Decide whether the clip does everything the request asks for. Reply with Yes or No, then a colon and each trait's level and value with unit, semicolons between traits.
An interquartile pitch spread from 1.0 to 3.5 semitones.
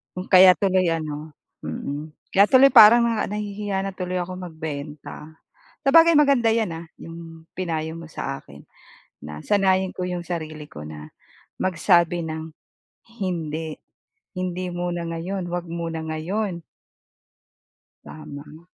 Yes: average, 3.2 semitones